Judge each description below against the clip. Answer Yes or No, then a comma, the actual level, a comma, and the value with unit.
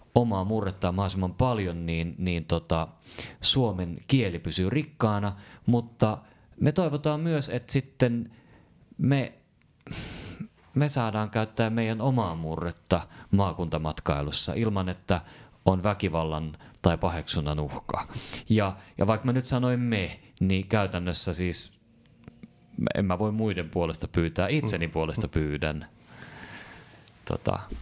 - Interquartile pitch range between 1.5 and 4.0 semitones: No, wide, 5.4 semitones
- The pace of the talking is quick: No, average, 110 wpm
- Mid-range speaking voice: No, low, 100 Hz